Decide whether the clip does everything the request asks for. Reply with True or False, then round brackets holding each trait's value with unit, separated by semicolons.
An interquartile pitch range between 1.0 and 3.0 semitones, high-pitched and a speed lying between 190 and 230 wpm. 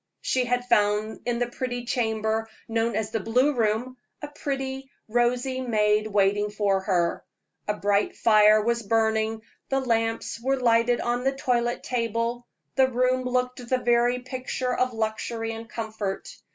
False (2.4 semitones; 235 Hz; 150 wpm)